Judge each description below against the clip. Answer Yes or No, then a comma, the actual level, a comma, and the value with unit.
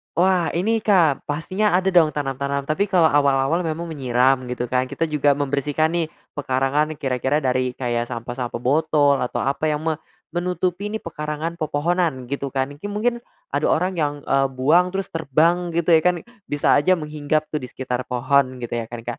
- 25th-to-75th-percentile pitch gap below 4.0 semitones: No, average, 4.3 semitones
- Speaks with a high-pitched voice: No, medium, 150 Hz